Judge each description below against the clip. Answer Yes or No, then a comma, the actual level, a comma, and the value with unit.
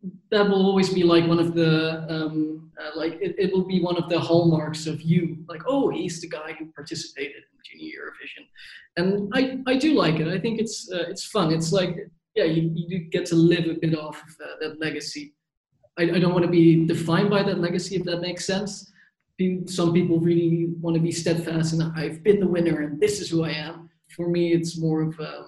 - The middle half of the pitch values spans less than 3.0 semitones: Yes, narrow, 2.5 semitones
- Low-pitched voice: No, medium, 170 Hz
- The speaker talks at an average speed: No, fast, 225 wpm